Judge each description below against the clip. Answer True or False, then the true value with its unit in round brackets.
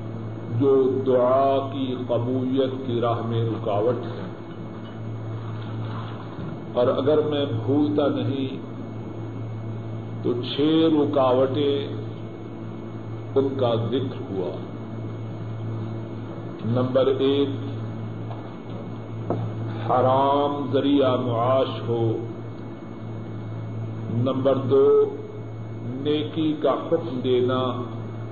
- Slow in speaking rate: True (70 wpm)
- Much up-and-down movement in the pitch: False (2.9 semitones)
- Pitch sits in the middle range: False (115 Hz)